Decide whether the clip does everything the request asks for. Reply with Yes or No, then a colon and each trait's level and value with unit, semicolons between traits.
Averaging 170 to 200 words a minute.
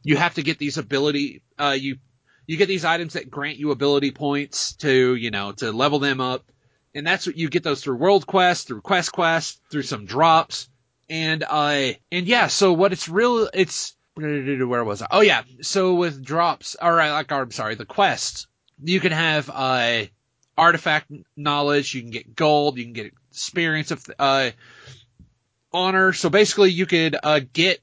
Yes: average, 190 wpm